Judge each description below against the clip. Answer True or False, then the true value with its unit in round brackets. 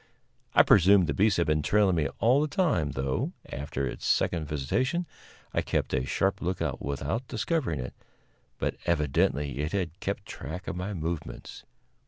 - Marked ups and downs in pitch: True (5.7 semitones)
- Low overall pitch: True (85 Hz)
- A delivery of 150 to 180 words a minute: True (165 wpm)